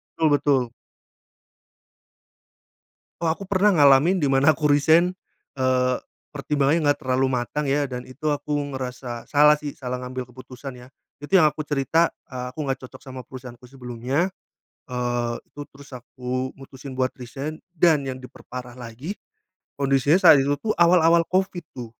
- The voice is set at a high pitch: No, low, 135 Hz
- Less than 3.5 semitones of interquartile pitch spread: Yes, average, 3.0 semitones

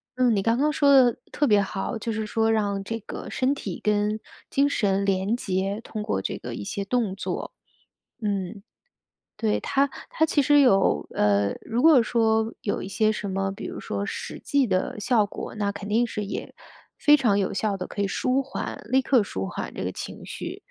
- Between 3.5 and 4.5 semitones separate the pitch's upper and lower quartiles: Yes, average, 3.9 semitones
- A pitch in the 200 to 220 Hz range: Yes, high, 215 Hz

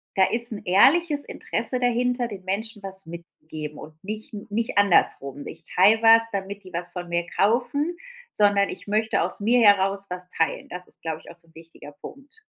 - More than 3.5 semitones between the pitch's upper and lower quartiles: Yes, average, 4.5 semitones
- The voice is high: Yes, high, 200 Hz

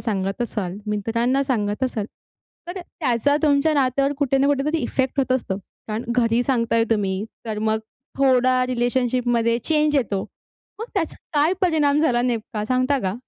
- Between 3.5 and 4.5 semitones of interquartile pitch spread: Yes, average, 3.8 semitones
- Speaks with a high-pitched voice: Yes, very high, 250 Hz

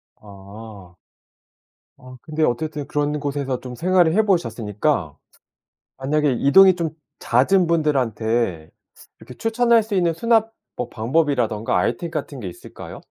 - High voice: No, medium, 145 Hz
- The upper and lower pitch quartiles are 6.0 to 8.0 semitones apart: Yes, wide, 6.6 semitones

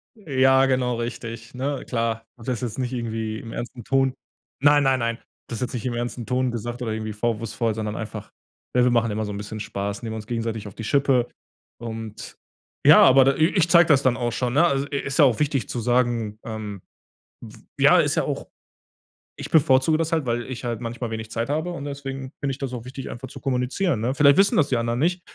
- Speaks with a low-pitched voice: Yes, low, 125 Hz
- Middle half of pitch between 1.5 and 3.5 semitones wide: Yes, average, 3.0 semitones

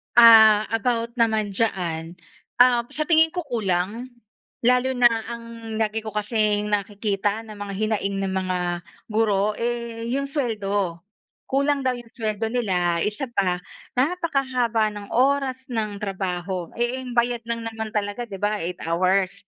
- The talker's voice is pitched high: Yes, high, 220 Hz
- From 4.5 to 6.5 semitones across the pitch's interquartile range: No, average, 3.3 semitones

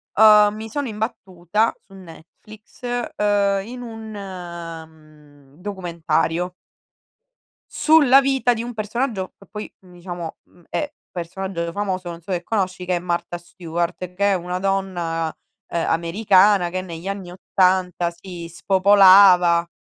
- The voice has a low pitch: No, medium, 185 Hz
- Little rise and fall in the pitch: No, average, 3.2 semitones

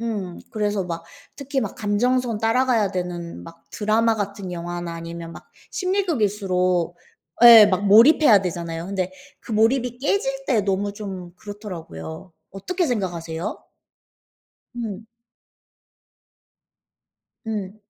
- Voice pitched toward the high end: Yes, high, 205 Hz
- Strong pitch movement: No, average, 4.4 semitones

